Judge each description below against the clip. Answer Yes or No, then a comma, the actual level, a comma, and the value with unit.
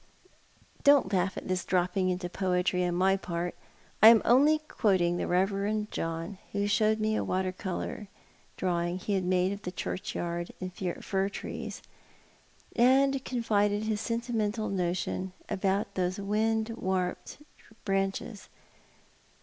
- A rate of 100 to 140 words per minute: Yes, slow, 135 wpm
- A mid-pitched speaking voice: No, high, 195 Hz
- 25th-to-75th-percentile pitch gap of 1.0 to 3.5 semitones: Yes, average, 3.1 semitones